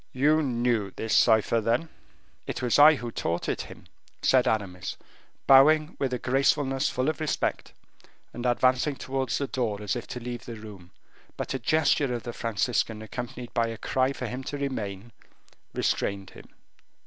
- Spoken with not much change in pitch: No, average, 3.2 semitones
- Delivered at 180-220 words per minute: No, average, 170 wpm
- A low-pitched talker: Yes, low, 125 Hz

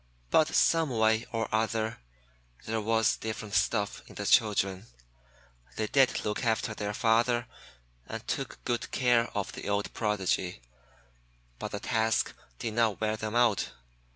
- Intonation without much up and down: Yes, narrow, 1.9 semitones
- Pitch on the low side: Yes, low, 110 Hz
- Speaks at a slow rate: No, average, 145 wpm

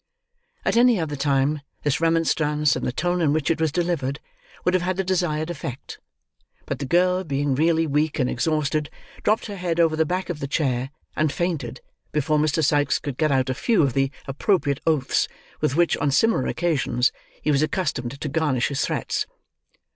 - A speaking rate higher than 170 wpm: Yes, average, 190 wpm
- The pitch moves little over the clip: No, average, 3.6 semitones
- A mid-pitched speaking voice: Yes, medium, 155 Hz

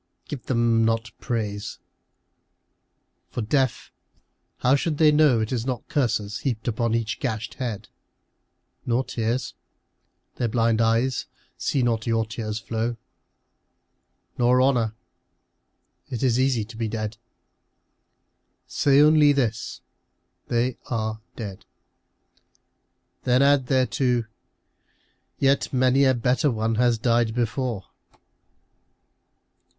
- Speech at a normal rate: No, slow, 115 wpm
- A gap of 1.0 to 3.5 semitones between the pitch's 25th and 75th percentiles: Yes, narrow, 2.6 semitones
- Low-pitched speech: Yes, low, 120 Hz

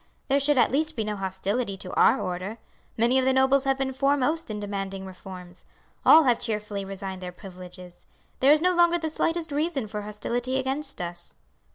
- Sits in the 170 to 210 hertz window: No, high, 230 Hz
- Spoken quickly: No, average, 190 wpm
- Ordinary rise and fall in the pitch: No, wide, 6.2 semitones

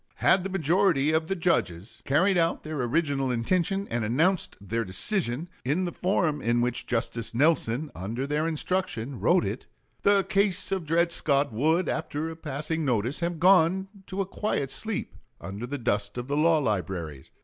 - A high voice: No, medium, 150 Hz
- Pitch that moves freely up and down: Yes, wide, 6.7 semitones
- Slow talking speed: No, average, 170 wpm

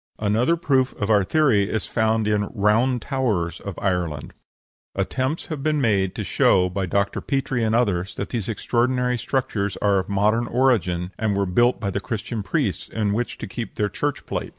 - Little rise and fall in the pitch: No, average, 3.9 semitones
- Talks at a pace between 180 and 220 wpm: Yes, average, 190 wpm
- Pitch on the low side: Yes, low, 110 Hz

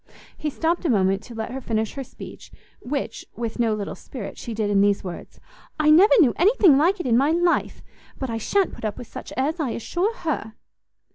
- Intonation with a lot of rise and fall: Yes, wide, 6.9 semitones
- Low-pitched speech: No, very high, 260 Hz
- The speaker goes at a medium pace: No, fast, 215 wpm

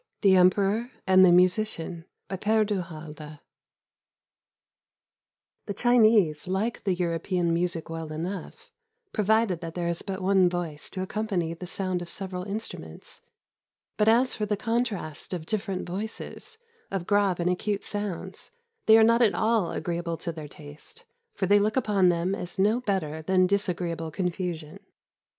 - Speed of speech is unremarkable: Yes, average, 155 wpm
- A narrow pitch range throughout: No, average, 3.6 semitones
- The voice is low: No, medium, 185 Hz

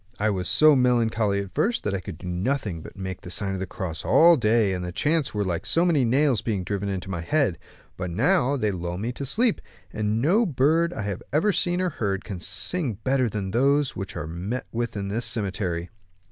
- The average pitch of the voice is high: No, low, 110 Hz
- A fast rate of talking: Yes, fast, 230 wpm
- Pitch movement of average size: No, wide, 6.8 semitones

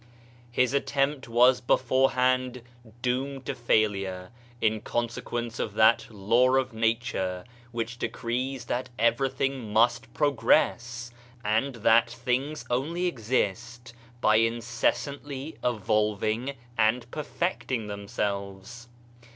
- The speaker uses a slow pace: Yes, slow, 95 wpm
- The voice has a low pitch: Yes, low, 120 Hz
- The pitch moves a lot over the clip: No, narrow, 2.6 semitones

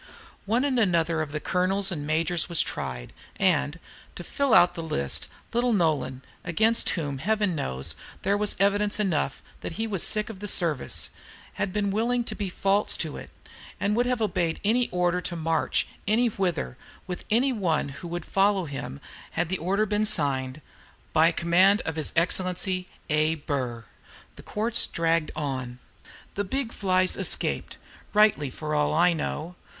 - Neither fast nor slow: Yes, average, 165 wpm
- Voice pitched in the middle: Yes, medium, 180 Hz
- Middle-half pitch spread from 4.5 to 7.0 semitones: Yes, average, 5.0 semitones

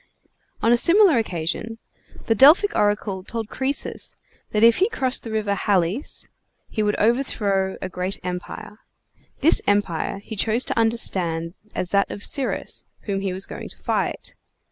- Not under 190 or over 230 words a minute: No, average, 155 wpm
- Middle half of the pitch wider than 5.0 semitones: No, average, 3.8 semitones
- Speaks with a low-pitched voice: No, high, 210 Hz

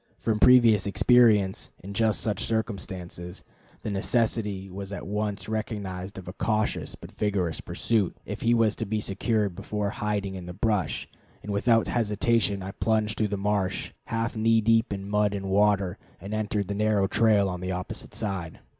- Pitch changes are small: Yes, narrow, 2.1 semitones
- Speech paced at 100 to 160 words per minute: No, average, 170 wpm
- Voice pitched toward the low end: Yes, low, 105 Hz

